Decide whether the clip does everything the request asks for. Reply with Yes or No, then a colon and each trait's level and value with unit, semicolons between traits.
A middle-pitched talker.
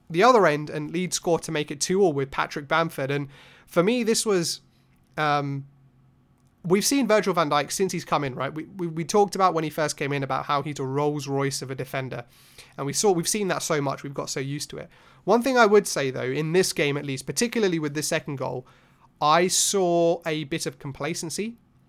Yes: medium, 155 Hz